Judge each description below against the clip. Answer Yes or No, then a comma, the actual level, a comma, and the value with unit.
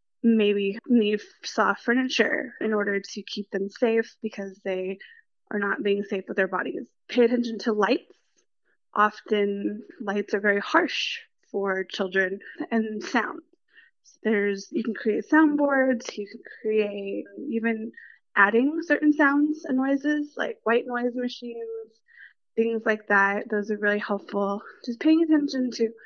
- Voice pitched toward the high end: Yes, high, 225 Hz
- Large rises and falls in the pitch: No, average, 3.9 semitones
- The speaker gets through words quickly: No, average, 145 wpm